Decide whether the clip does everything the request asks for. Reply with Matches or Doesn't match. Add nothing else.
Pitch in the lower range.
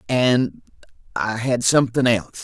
Matches